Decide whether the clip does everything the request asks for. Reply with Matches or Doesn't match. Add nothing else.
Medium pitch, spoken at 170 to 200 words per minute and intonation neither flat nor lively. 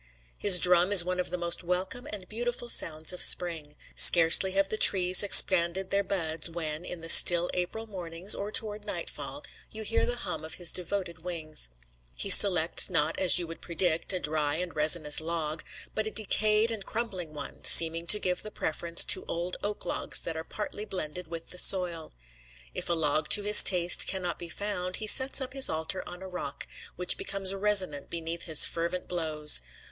Matches